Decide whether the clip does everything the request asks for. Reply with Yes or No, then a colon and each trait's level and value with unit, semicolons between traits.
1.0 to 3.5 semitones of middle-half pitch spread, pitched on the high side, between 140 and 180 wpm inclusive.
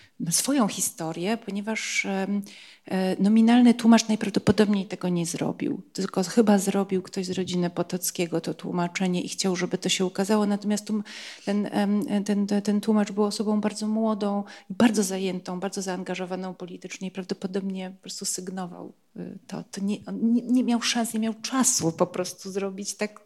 Yes: narrow, 2.4 semitones; high, 200 Hz; average, 145 wpm